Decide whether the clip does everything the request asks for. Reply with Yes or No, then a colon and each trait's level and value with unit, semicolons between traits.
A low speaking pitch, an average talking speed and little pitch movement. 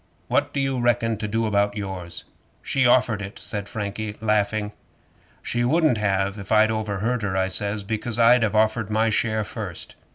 Yes: low, 110 Hz; average, 175 wpm; narrow, 2.1 semitones